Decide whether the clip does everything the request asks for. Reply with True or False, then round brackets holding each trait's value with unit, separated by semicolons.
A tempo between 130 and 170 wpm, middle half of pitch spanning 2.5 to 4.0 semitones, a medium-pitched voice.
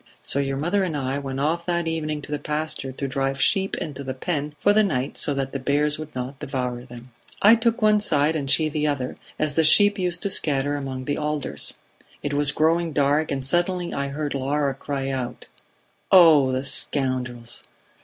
False (205 wpm; 3.1 semitones; 145 Hz)